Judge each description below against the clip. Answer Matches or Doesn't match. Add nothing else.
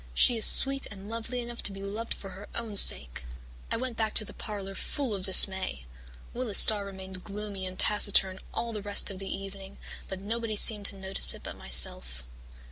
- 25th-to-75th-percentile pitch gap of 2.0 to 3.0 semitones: Matches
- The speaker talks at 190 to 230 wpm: Matches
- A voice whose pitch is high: Matches